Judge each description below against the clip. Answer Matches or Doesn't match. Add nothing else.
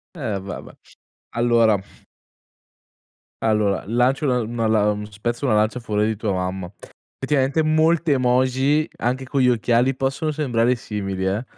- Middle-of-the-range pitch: Doesn't match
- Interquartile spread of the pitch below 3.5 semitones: Doesn't match